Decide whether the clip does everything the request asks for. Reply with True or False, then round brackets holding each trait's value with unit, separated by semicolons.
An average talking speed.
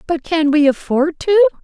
True (185 wpm)